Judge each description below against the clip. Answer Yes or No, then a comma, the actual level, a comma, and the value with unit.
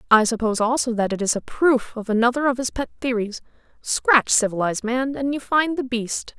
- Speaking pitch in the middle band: No, high, 240 Hz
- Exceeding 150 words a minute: Yes, fast, 205 wpm